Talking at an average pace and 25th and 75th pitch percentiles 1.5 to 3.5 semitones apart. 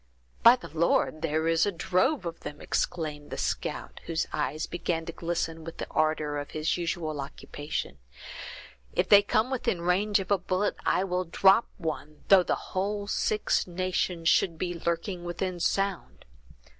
Yes: average, 165 wpm; average, 3.1 semitones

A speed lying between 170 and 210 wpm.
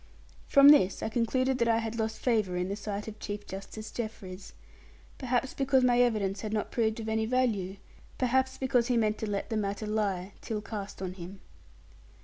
Yes: average, 190 wpm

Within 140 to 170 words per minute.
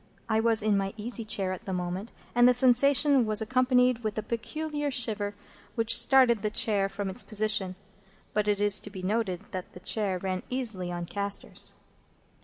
No: average, 185 wpm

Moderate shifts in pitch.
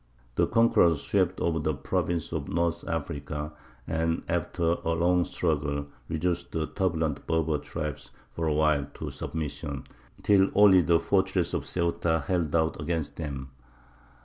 No: narrow, 2.2 semitones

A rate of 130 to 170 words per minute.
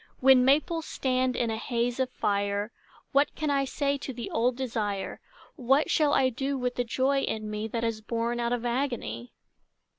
No: average, 185 wpm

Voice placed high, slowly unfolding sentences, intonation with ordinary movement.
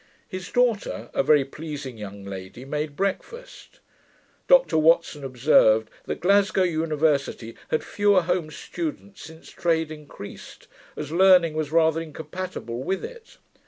No: medium, 160 Hz; slow, 125 wpm; average, 4.7 semitones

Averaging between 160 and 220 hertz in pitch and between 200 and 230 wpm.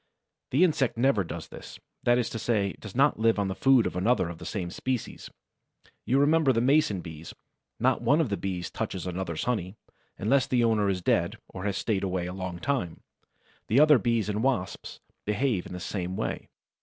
No: low, 105 Hz; fast, 205 wpm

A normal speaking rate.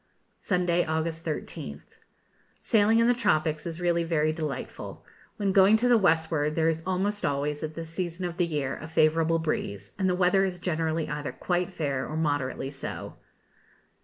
Yes: average, 170 wpm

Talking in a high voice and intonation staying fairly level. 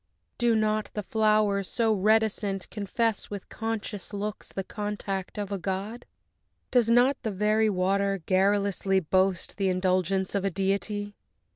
Yes: high, 200 Hz; narrow, 1.9 semitones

